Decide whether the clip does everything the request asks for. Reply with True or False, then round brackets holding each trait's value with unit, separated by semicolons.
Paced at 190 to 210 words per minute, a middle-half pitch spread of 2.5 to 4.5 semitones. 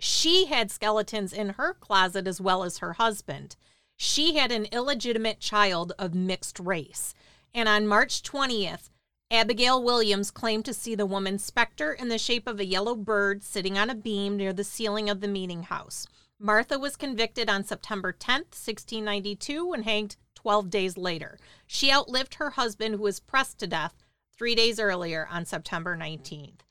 False (170 wpm; 3.5 semitones)